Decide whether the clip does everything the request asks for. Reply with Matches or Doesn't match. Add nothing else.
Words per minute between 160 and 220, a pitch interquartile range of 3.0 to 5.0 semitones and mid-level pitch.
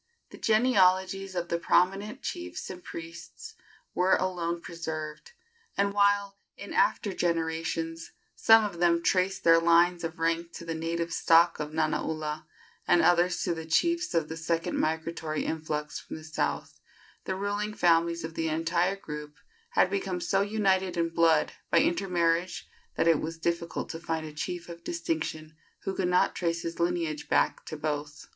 Doesn't match